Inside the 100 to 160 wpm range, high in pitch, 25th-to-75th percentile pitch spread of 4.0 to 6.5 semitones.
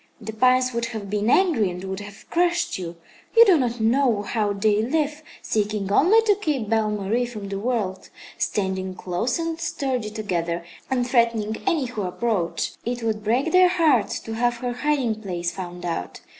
No: average, 180 wpm; high, 225 Hz; average, 4.4 semitones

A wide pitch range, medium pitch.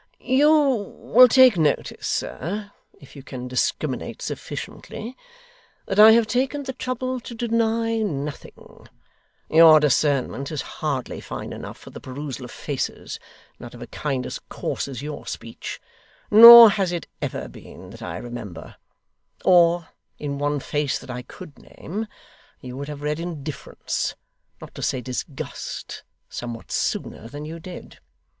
Yes: wide, 8.3 semitones; medium, 160 Hz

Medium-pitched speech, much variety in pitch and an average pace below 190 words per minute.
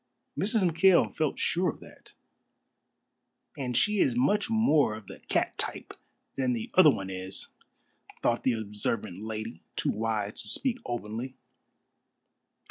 No: low, 120 Hz; wide, 8.0 semitones; slow, 135 wpm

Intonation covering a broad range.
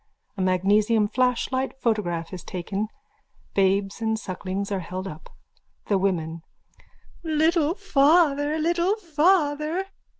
Yes: wide, 8.3 semitones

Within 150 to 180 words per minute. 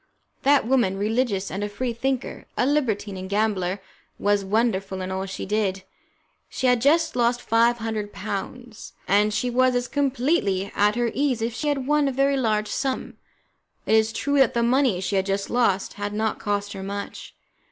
No: average, 190 wpm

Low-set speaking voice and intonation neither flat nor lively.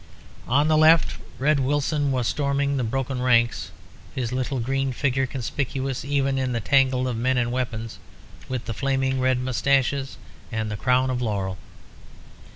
No: low, 130 Hz; narrow, 2.0 semitones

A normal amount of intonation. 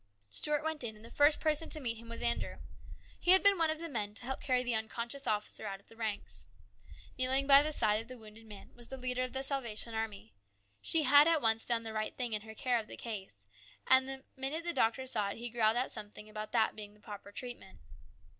Yes: average, 3.8 semitones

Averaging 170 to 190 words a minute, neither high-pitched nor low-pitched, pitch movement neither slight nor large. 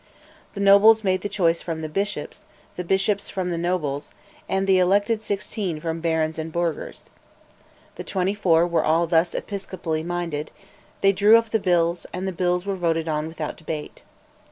Yes: average, 180 wpm; medium, 175 Hz; average, 3.2 semitones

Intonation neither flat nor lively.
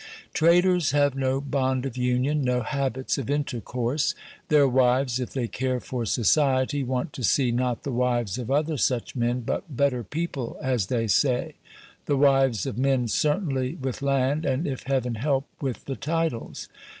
No: narrow, 2.2 semitones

